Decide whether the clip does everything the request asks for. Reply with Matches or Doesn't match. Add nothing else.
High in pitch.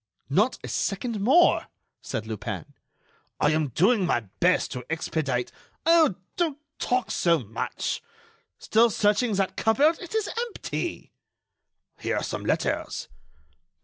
Matches